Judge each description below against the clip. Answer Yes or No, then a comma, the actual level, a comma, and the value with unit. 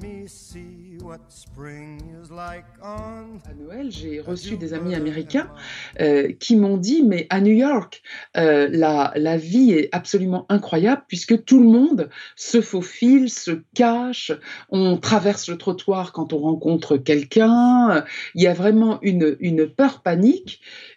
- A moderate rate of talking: No, slow, 120 wpm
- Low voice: No, medium, 185 Hz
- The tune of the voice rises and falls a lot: Yes, wide, 5.9 semitones